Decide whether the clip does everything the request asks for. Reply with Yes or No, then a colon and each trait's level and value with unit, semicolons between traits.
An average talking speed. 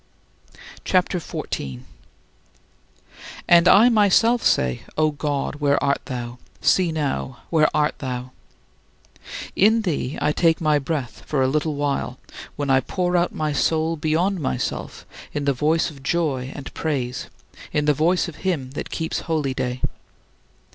Yes: average, 150 wpm